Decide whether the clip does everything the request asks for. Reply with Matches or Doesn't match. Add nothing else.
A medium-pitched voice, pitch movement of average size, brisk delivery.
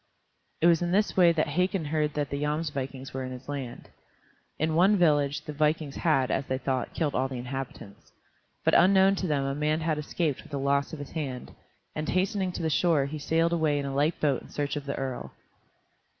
Matches